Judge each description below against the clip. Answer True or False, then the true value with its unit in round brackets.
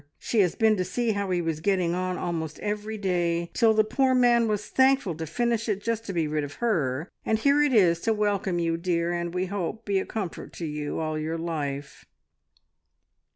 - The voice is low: False (185 Hz)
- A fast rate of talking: True (215 wpm)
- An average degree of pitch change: True (4.7 semitones)